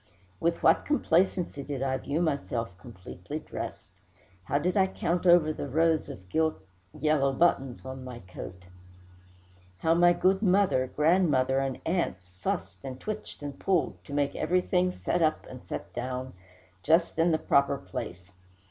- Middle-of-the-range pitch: Yes, medium, 145 Hz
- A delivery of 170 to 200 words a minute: No, average, 155 wpm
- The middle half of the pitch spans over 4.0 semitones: Yes, average, 5.0 semitones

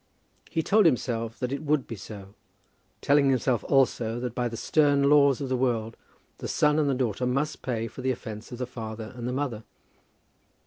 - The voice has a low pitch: Yes, low, 125 Hz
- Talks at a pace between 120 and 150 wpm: No, average, 195 wpm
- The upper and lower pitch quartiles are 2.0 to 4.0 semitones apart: Yes, average, 3.5 semitones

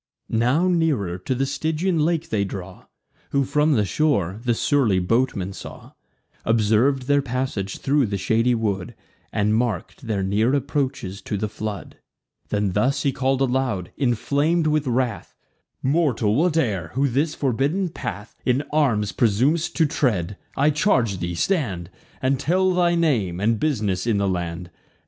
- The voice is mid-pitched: No, low, 125 Hz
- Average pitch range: No, wide, 6.0 semitones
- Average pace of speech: Yes, average, 150 wpm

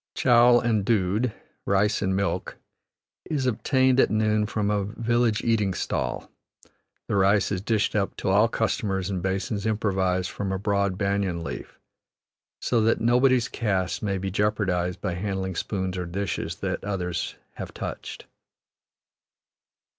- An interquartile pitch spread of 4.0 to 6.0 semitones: No, average, 2.8 semitones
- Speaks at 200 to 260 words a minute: No, average, 140 wpm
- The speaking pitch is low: Yes, low, 100 Hz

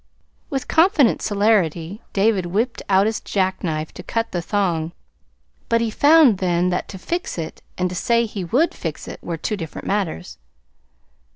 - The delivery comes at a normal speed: Yes, average, 165 wpm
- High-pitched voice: Yes, high, 195 Hz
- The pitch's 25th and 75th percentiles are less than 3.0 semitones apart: No, average, 4.7 semitones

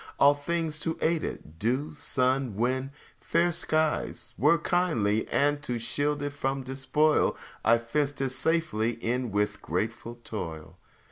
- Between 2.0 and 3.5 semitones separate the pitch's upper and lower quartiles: No, average, 4.4 semitones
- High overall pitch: No, low, 135 Hz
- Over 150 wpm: No, average, 140 wpm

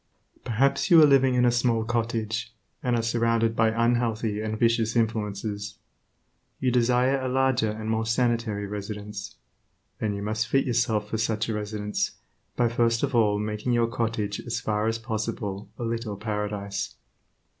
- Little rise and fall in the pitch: Yes, narrow, 2.0 semitones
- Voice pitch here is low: Yes, low, 115 Hz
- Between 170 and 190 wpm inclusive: No, average, 160 wpm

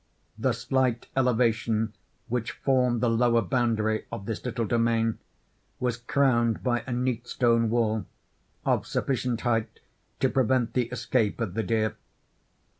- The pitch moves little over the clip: Yes, narrow, 1.7 semitones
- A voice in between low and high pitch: No, low, 115 Hz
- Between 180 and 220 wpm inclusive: No, slow, 135 wpm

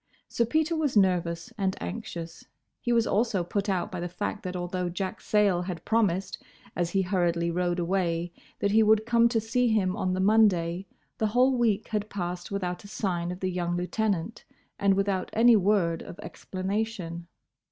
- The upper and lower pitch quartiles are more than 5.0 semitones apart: No, average, 3.7 semitones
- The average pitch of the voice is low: No, high, 190 Hz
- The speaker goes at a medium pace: Yes, average, 180 wpm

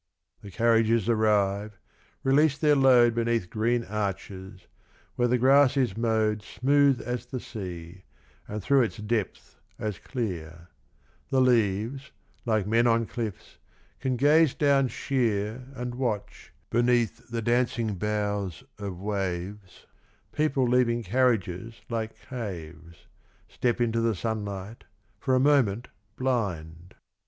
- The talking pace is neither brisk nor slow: No, slow, 120 wpm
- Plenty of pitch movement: No, average, 3.7 semitones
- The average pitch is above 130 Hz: No, low, 115 Hz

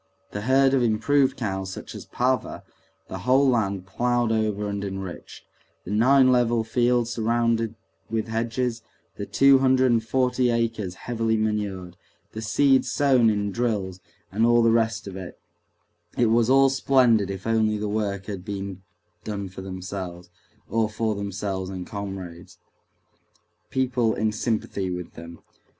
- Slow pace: No, average, 145 wpm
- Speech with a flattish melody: No, average, 3.5 semitones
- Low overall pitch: Yes, low, 110 Hz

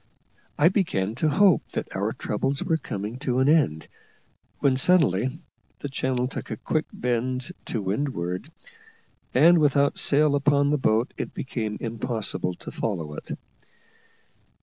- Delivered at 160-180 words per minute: No, average, 140 wpm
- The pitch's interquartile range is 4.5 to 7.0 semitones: Yes, average, 5.2 semitones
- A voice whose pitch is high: No, low, 130 Hz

